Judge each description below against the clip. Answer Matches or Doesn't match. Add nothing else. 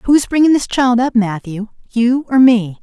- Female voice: Matches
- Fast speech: Doesn't match